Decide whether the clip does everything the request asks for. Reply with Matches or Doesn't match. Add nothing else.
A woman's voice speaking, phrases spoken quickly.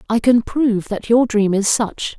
Matches